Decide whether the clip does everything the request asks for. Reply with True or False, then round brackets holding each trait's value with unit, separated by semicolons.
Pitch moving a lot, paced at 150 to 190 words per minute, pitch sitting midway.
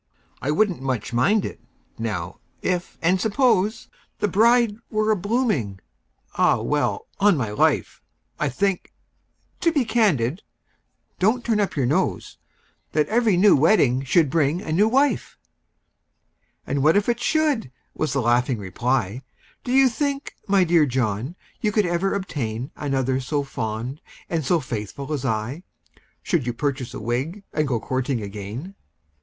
False (8.6 semitones; 140 wpm; 155 Hz)